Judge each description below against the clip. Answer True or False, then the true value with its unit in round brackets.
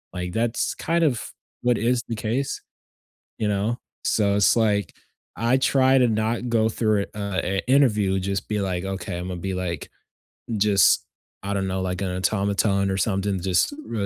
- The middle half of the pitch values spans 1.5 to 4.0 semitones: True (3.2 semitones)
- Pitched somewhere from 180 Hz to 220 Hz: False (100 Hz)